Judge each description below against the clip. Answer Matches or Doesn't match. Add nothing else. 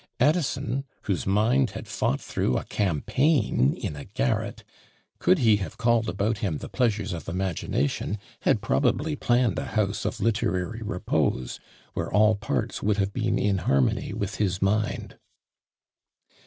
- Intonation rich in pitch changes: Doesn't match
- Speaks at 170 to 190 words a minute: Doesn't match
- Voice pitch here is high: Doesn't match